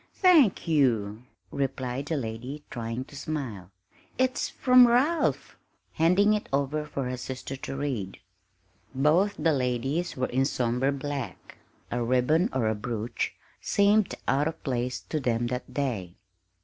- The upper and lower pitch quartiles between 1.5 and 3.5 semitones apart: No, average, 4.5 semitones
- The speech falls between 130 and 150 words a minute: Yes, average, 140 wpm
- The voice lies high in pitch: No, low, 135 Hz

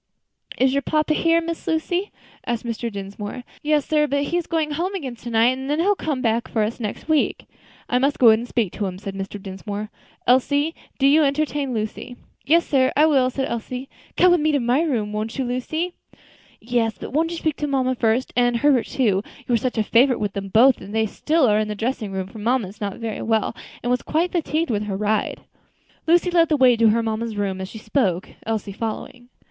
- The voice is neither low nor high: No, very high, 250 Hz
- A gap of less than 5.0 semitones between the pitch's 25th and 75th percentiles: No, average, 5.3 semitones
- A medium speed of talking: No, fast, 230 wpm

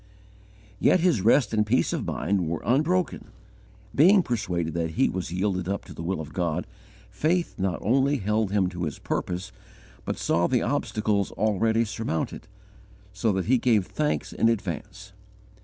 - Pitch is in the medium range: No, low, 105 Hz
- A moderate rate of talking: Yes, average, 160 wpm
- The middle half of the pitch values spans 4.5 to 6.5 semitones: Yes, average, 5.0 semitones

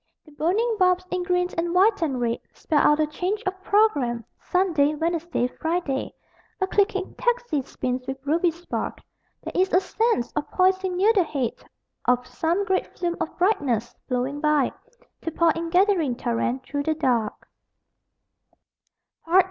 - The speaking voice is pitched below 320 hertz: No, very high, 330 Hz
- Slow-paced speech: No, average, 155 wpm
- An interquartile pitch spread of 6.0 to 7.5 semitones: No, wide, 5.5 semitones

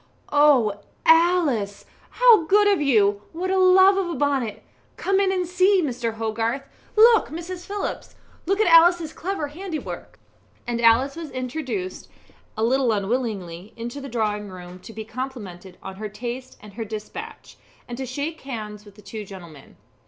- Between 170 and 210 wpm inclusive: No, average, 160 wpm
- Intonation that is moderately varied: No, wide, 8.3 semitones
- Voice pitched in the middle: No, very high, 255 Hz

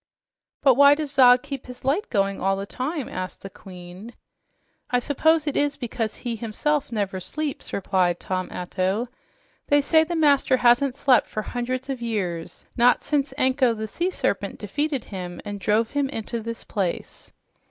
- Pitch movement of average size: No, wide, 5.9 semitones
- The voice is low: No, high, 245 Hz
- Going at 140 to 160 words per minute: No, average, 170 wpm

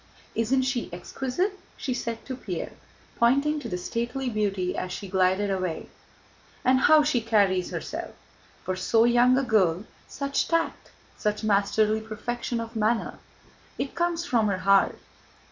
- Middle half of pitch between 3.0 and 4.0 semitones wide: No, average, 4.6 semitones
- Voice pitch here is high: Yes, high, 225 Hz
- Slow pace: No, average, 145 wpm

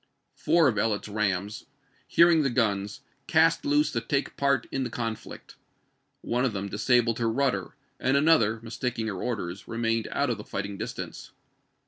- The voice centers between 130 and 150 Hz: No, low, 115 Hz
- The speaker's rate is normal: Yes, average, 155 wpm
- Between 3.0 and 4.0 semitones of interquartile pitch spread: No, average, 4.4 semitones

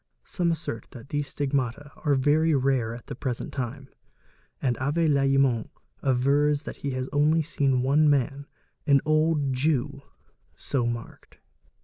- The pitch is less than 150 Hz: Yes, medium, 140 Hz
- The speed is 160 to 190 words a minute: No, average, 140 wpm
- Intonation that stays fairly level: Yes, narrow, 2.2 semitones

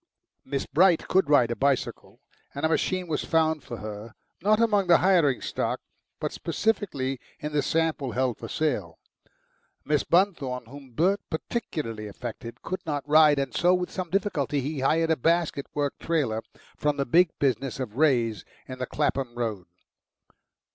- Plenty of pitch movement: No, average, 4.7 semitones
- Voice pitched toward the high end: No, medium, 145 Hz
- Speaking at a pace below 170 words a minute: Yes, average, 160 wpm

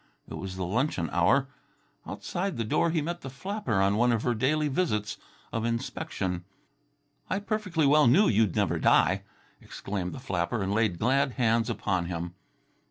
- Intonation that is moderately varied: No, wide, 7.6 semitones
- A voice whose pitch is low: Yes, low, 115 Hz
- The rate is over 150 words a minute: Yes, average, 165 wpm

